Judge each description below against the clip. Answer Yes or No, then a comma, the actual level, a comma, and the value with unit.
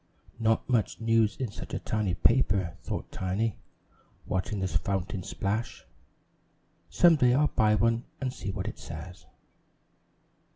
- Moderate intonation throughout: Yes, average, 3.6 semitones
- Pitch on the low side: Yes, low, 105 Hz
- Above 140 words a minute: No, slow, 135 wpm